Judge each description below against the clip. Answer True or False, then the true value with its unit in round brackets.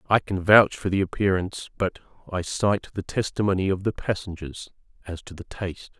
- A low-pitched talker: True (95 Hz)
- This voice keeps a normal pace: True (180 wpm)